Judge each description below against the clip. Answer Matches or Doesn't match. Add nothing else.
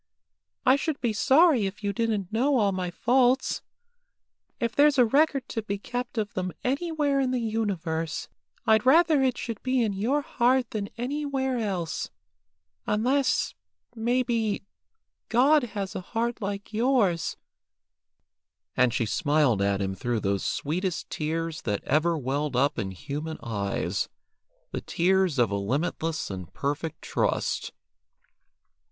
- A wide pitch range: Matches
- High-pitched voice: Matches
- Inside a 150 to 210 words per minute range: Doesn't match